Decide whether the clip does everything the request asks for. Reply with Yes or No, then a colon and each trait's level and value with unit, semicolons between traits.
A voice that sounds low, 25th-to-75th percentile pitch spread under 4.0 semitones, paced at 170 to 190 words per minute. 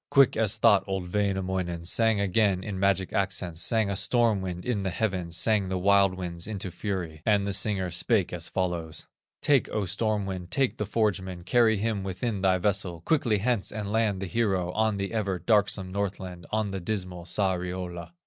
Yes: very low, 95 Hz; average, 2.7 semitones; average, 185 wpm